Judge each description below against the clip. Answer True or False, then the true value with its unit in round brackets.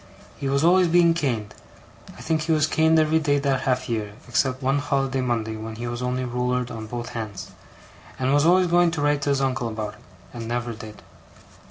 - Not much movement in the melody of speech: False (4.1 semitones)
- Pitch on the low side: True (130 Hz)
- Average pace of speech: False (210 wpm)